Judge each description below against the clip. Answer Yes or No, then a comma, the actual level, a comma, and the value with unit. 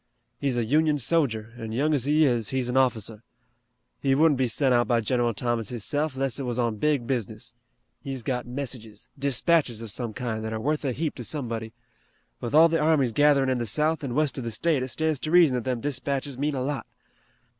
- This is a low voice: Yes, low, 130 Hz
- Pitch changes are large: No, average, 3.7 semitones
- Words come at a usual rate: No, fast, 220 wpm